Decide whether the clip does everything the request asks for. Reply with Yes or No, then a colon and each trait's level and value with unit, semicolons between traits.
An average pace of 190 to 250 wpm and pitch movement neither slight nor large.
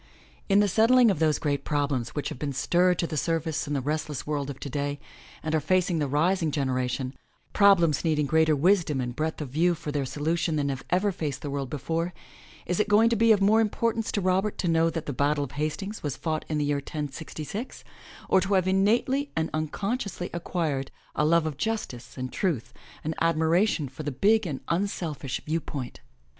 Yes: fast, 205 wpm; average, 4.6 semitones